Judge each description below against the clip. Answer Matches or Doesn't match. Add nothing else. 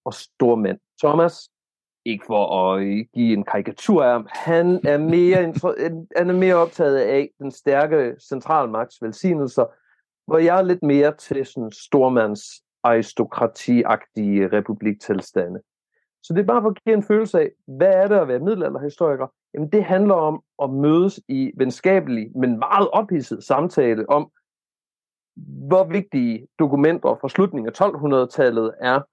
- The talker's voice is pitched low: Doesn't match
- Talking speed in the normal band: Doesn't match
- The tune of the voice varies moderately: Doesn't match